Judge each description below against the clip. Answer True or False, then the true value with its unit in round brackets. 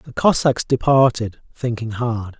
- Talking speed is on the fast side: False (125 wpm)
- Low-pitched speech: True (120 Hz)